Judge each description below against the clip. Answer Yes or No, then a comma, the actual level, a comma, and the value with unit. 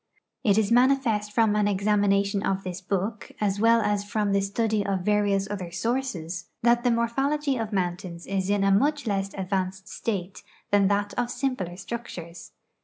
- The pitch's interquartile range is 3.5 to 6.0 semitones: No, average, 2.9 semitones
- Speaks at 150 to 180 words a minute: Yes, average, 170 wpm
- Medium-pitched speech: No, high, 205 Hz